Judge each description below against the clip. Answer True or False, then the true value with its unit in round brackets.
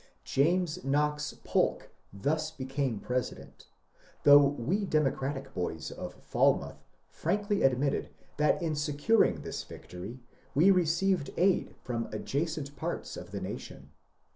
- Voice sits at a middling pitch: True (145 Hz)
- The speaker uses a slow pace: True (115 wpm)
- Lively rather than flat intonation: False (3.6 semitones)